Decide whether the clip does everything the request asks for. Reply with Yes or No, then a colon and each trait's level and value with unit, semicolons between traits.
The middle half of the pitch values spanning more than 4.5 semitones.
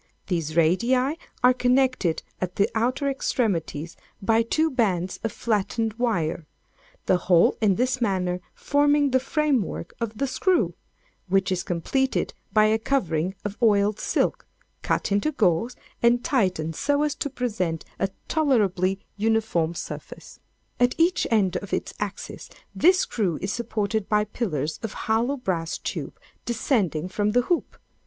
Yes: wide, 5.5 semitones